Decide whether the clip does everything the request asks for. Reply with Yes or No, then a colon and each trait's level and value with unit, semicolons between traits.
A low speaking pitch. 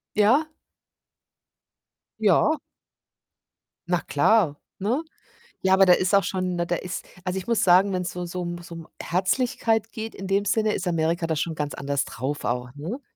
No: medium, 185 Hz